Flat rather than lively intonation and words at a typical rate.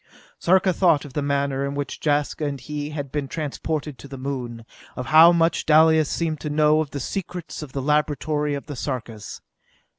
Yes: narrow, 2.0 semitones; average, 190 wpm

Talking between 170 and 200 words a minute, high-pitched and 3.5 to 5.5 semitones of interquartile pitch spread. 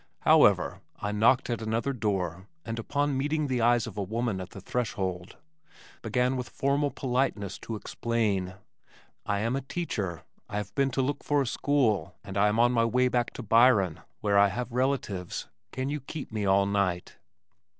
No: average, 180 wpm; low, 115 Hz; average, 4.5 semitones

